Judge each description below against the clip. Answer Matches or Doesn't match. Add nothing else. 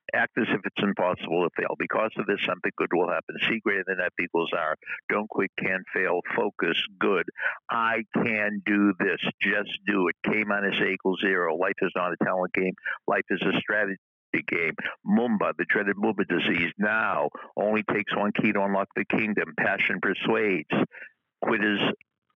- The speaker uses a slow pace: Doesn't match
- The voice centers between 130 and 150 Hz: Doesn't match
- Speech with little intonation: Matches